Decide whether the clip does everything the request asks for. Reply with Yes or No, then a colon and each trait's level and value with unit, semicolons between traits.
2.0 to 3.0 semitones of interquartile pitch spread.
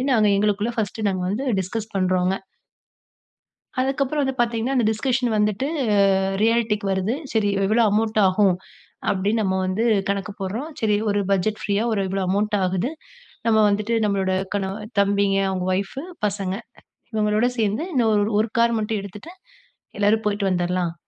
Yes: narrow, 2.5 semitones